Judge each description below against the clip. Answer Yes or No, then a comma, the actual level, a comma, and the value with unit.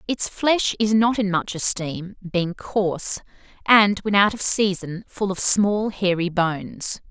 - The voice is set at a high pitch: Yes, high, 195 Hz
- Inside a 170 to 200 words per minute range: No, average, 160 wpm